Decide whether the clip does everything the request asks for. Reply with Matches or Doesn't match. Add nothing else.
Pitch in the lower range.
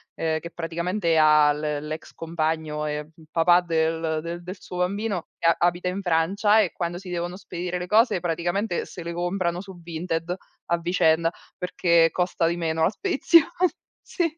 Doesn't match